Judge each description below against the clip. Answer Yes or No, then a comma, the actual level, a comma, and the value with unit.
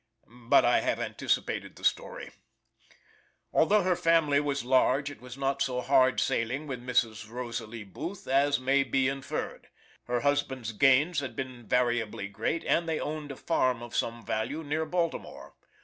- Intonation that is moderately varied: Yes, average, 3.3 semitones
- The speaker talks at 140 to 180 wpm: Yes, average, 160 wpm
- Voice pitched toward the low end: Yes, low, 130 Hz